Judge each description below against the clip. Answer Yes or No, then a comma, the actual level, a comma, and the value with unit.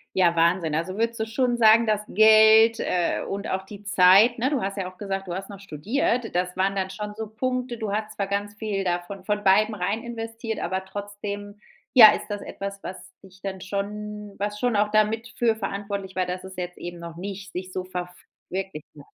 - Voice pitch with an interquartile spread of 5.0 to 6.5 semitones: No, narrow, 2.6 semitones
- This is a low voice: No, high, 200 Hz